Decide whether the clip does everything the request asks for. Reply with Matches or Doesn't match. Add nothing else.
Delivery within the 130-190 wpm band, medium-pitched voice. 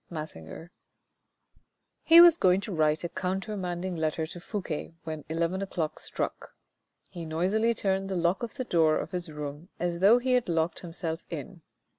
Matches